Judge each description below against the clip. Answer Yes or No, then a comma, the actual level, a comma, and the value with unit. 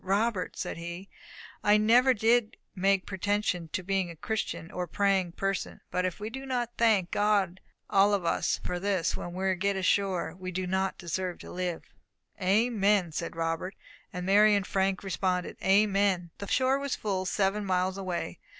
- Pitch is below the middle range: No, high, 195 Hz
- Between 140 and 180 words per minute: Yes, average, 175 wpm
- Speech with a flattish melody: Yes, narrow, 2.3 semitones